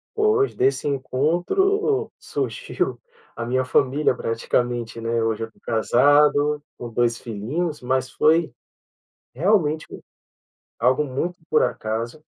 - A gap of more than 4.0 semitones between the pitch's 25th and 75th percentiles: Yes, average, 5.1 semitones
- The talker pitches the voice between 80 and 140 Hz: Yes, low, 135 Hz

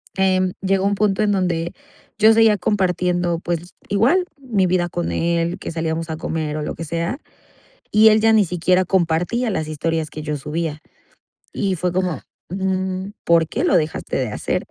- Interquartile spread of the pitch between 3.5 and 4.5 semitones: No, average, 3.0 semitones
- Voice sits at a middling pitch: Yes, medium, 180 Hz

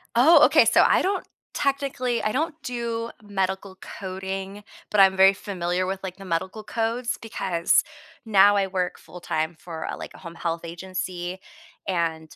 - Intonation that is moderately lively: Yes, average, 4.0 semitones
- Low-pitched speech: No, high, 190 Hz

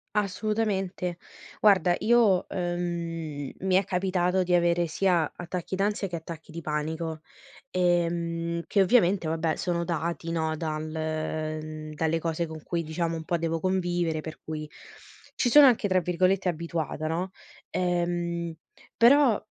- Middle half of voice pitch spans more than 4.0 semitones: No, narrow, 2.5 semitones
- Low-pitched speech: No, medium, 170 Hz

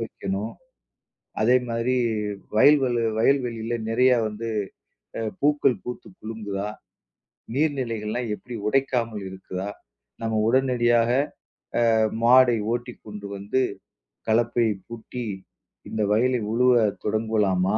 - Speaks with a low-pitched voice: Yes, low, 115 Hz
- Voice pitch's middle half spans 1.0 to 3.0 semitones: Yes, narrow, 2.5 semitones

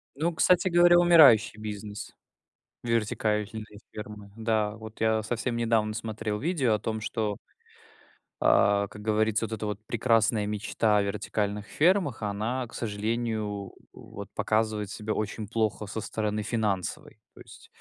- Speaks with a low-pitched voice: Yes, low, 110 Hz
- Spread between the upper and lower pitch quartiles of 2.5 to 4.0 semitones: No, narrow, 1.7 semitones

